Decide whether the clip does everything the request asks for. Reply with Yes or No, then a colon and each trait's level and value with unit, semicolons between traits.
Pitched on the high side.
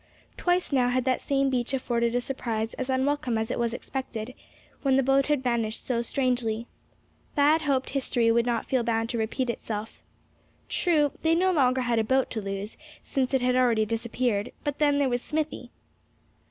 Yes: very high, 250 Hz